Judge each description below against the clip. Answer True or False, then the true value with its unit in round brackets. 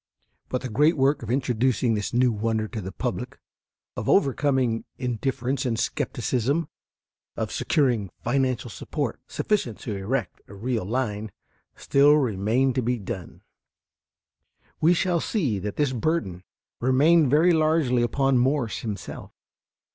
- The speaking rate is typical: False (130 wpm)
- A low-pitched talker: True (125 Hz)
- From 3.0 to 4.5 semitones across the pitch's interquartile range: True (4.1 semitones)